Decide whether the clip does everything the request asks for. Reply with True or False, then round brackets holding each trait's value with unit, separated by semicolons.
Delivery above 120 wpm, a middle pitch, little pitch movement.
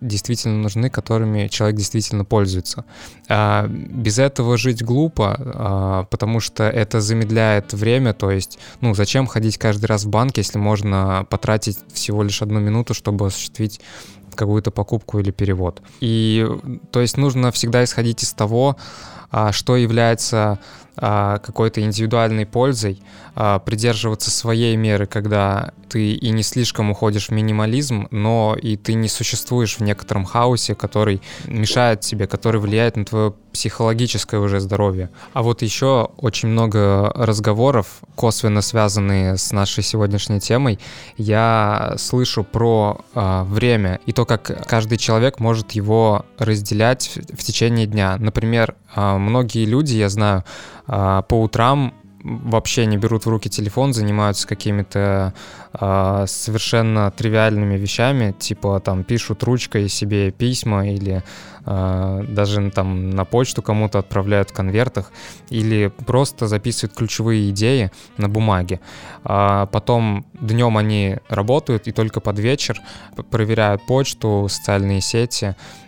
False (130 wpm; 110 Hz; 2.3 semitones)